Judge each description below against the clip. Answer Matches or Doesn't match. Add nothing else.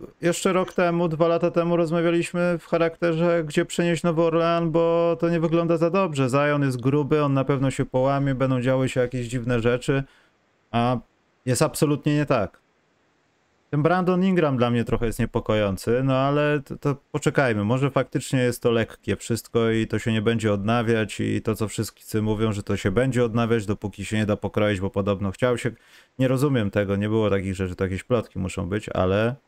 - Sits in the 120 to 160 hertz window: Matches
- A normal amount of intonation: Doesn't match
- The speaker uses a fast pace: Matches